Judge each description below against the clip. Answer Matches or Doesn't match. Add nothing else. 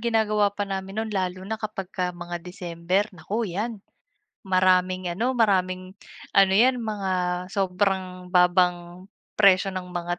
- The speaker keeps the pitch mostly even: Matches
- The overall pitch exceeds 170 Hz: Matches